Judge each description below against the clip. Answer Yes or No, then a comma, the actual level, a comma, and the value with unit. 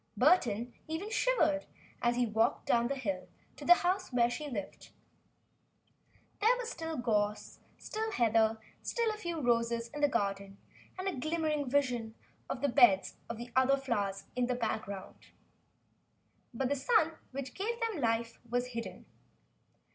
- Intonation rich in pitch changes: Yes, wide, 5.8 semitones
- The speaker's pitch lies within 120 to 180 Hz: No, very high, 250 Hz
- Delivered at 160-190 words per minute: No, average, 150 wpm